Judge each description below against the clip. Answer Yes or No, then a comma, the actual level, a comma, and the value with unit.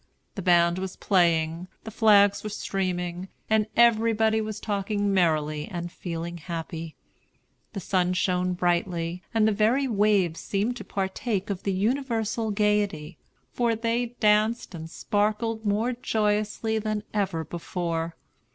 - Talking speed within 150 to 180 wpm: No, slow, 135 wpm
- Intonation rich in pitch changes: No, average, 3.8 semitones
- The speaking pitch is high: Yes, high, 200 Hz